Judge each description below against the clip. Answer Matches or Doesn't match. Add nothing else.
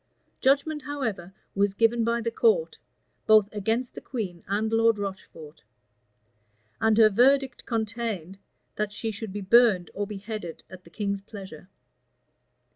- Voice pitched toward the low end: Doesn't match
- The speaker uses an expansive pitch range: Doesn't match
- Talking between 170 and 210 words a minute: Doesn't match